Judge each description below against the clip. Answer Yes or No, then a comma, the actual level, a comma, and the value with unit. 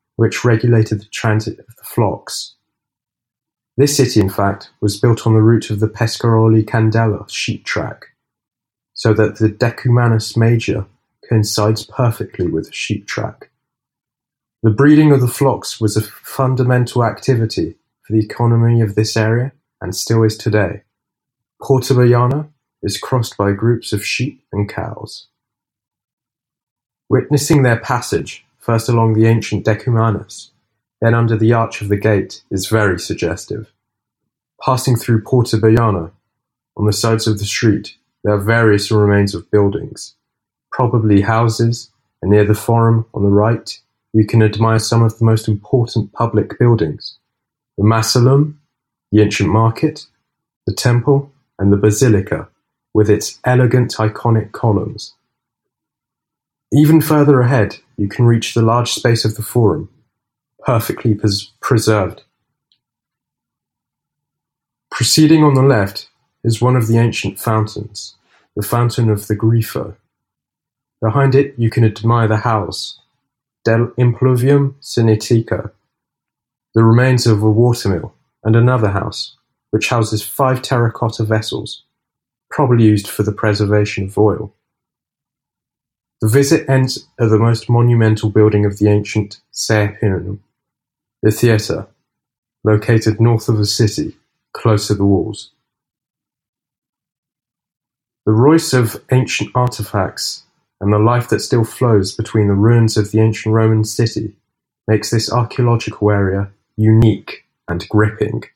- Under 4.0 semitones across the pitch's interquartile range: Yes, narrow, 2.5 semitones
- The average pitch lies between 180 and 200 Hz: No, low, 115 Hz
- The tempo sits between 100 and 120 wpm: No, average, 130 wpm